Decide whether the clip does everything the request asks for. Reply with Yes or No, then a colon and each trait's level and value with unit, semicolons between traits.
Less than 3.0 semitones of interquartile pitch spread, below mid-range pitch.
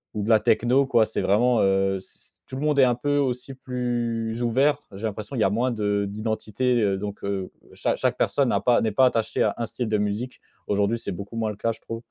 No: average, 3.3 semitones; low, 115 Hz